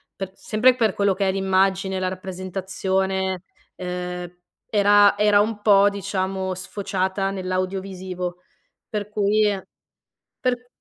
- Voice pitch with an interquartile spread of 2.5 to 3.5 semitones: No, narrow, 1.4 semitones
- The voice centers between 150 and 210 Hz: Yes, high, 190 Hz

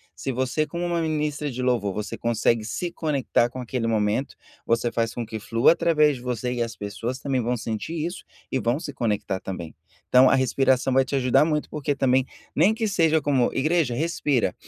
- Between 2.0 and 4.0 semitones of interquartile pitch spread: No, average, 4.5 semitones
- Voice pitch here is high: No, low, 130 Hz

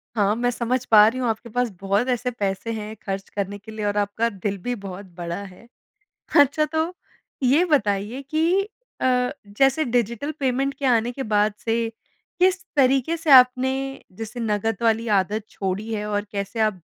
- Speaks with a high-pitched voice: Yes, high, 225 Hz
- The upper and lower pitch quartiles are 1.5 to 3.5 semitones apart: No, average, 3.9 semitones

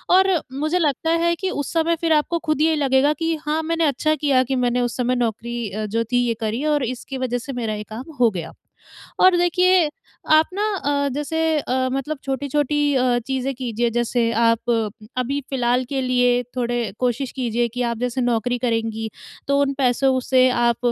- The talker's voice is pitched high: Yes, very high, 260 Hz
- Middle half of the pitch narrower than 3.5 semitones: No, average, 3.8 semitones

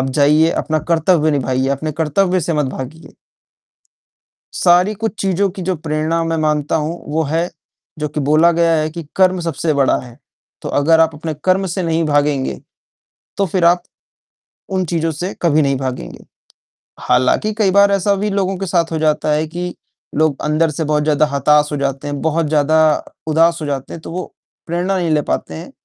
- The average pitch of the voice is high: No, medium, 160 Hz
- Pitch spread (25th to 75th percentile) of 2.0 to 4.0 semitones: Yes, average, 2.8 semitones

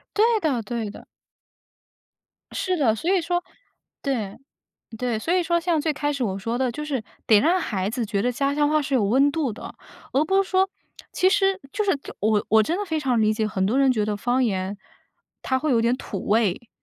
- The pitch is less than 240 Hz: No, very high, 260 Hz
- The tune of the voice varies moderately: No, wide, 6.7 semitones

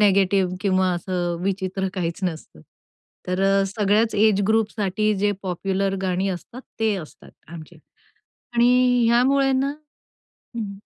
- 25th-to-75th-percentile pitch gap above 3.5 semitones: No, average, 2.9 semitones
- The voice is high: Yes, high, 195 Hz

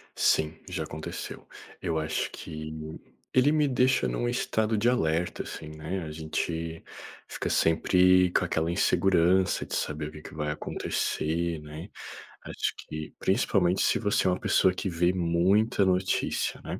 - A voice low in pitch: Yes, very low, 85 Hz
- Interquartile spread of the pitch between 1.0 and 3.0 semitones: No, average, 3.4 semitones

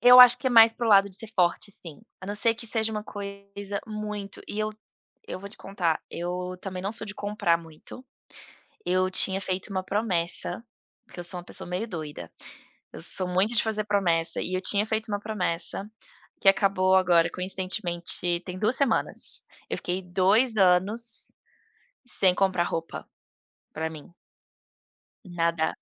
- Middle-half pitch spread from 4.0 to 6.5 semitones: No, average, 3.0 semitones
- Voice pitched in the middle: No, high, 195 Hz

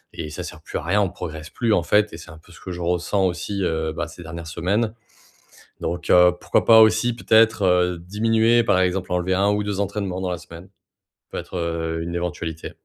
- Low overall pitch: Yes, very low, 90 Hz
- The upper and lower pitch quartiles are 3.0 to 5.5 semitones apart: Yes, average, 3.4 semitones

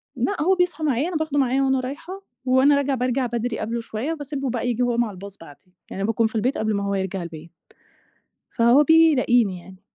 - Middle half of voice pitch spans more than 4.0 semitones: Yes, average, 4.9 semitones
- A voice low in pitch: No, high, 245 Hz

